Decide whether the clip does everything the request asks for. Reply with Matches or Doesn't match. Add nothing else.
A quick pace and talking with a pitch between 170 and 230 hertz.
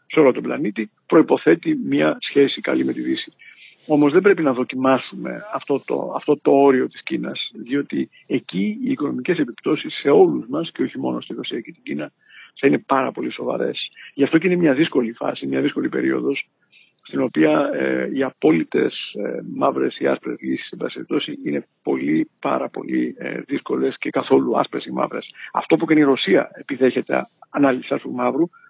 Doesn't match